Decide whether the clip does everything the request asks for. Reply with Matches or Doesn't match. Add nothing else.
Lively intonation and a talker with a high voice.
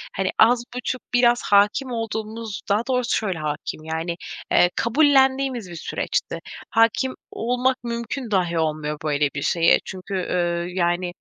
Matches